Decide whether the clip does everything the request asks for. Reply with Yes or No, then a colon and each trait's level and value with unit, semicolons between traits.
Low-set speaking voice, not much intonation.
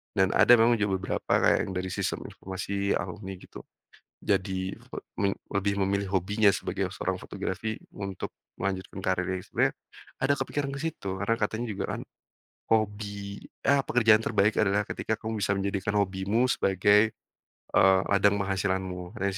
Yes: low, 100 Hz; narrow, 2.1 semitones